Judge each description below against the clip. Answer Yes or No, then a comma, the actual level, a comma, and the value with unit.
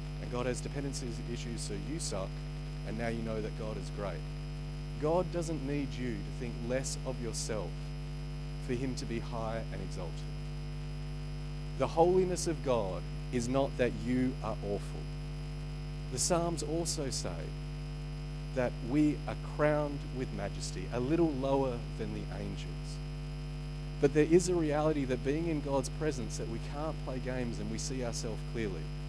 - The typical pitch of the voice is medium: Yes, medium, 150 Hz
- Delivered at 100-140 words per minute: No, average, 160 wpm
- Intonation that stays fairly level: Yes, narrow, 1.1 semitones